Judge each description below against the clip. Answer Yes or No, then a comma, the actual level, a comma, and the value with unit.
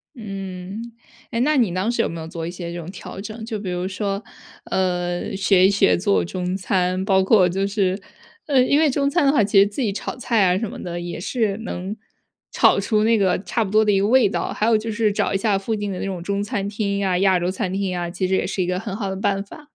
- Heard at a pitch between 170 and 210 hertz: Yes, high, 195 Hz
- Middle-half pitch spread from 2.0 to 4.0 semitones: Yes, average, 2.9 semitones